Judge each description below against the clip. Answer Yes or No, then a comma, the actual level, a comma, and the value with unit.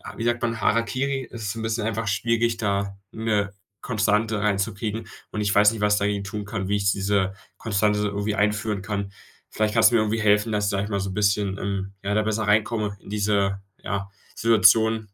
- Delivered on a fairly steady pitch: Yes, narrow, 1.8 semitones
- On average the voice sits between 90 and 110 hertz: Yes, low, 105 Hz